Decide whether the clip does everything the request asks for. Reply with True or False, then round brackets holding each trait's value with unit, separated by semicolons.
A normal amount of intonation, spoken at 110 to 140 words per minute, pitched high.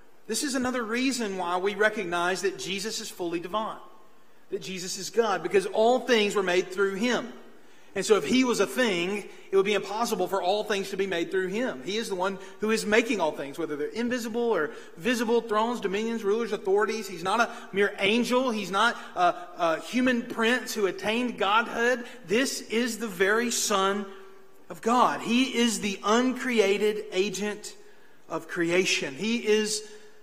False (3.3 semitones; 180 wpm; 210 Hz)